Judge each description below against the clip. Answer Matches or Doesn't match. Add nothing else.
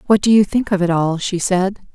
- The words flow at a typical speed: Doesn't match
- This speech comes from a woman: Matches